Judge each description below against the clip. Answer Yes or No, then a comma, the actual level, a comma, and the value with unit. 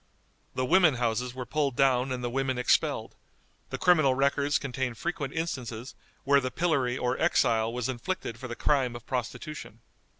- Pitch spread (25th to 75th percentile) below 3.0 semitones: Yes, narrow, 2.6 semitones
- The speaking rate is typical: Yes, average, 165 wpm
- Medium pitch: No, low, 130 Hz